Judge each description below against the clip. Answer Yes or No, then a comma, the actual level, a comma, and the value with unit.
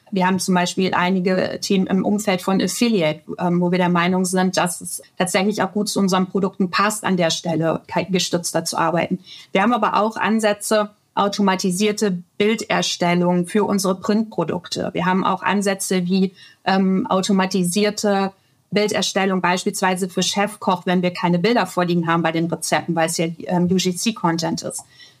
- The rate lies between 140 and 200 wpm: Yes, average, 155 wpm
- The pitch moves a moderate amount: No, narrow, 2.2 semitones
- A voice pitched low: No, medium, 185 Hz